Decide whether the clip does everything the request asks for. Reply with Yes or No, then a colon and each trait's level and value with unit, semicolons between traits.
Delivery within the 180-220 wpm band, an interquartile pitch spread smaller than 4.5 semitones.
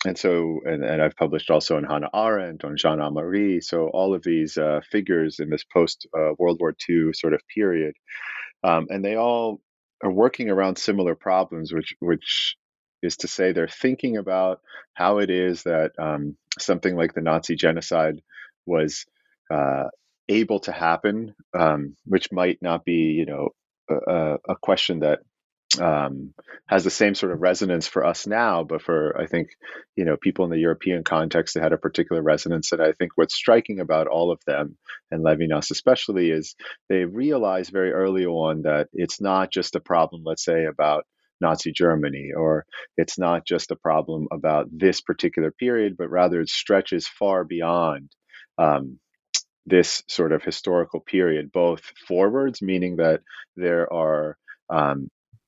No: average, 170 wpm; average, 3.1 semitones